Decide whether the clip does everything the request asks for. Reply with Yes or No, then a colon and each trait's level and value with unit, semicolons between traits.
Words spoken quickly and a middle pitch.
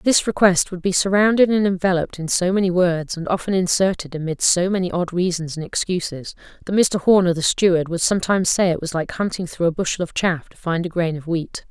Yes: fast, 225 wpm; medium, 180 Hz